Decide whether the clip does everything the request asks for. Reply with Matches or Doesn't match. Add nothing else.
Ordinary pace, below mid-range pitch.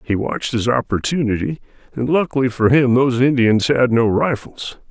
Matches